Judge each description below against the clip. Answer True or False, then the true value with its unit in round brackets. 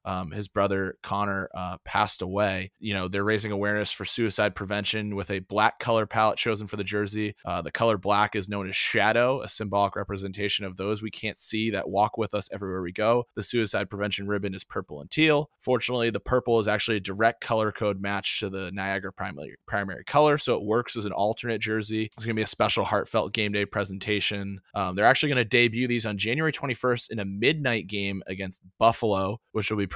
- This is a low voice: True (105 Hz)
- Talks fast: True (215 wpm)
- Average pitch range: False (2.2 semitones)